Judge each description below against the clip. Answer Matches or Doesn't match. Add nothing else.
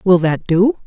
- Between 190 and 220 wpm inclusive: Matches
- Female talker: Matches